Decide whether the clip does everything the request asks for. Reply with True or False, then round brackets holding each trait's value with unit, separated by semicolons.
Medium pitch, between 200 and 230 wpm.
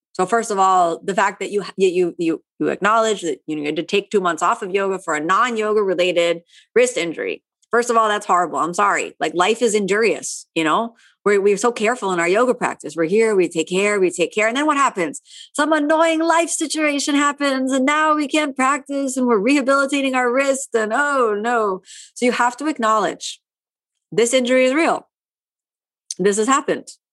False (225 Hz; 205 wpm)